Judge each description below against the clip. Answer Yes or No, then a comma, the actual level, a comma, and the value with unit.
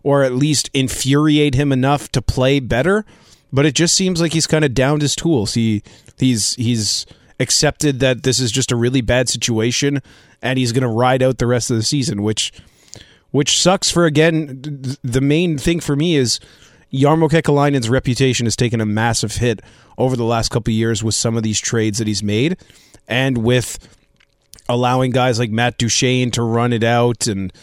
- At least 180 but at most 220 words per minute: Yes, average, 195 wpm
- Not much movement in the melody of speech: No, average, 3.6 semitones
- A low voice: Yes, low, 125 Hz